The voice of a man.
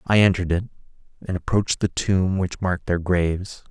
Yes: male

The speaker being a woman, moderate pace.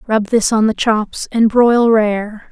Yes: female; average, 190 wpm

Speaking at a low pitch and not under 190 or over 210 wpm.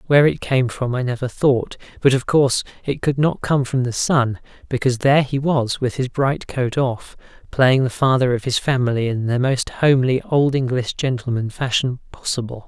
Yes: low, 130 Hz; average, 195 wpm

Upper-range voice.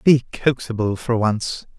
No: low, 115 Hz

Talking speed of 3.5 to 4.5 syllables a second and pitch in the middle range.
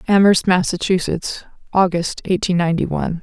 No: 5.5 syllables/s; medium, 180 Hz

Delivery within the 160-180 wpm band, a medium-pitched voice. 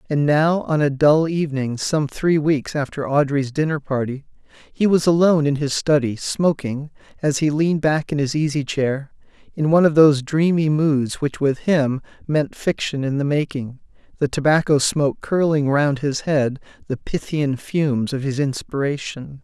Yes: average, 170 wpm; medium, 145 Hz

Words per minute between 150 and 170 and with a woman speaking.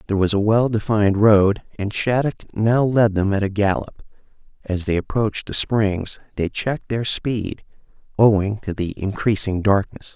No: average, 165 wpm; male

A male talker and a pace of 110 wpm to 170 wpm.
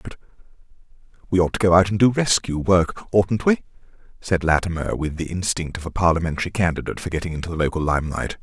No: male; average, 190 wpm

